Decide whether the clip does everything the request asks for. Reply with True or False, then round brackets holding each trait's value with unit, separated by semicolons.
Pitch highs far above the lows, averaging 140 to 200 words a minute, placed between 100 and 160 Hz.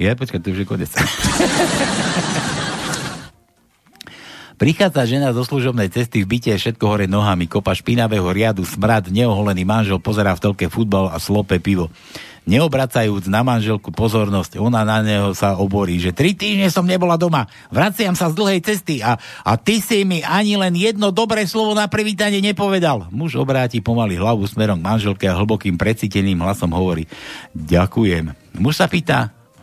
True (8.5 semitones; 160 wpm; 110 Hz)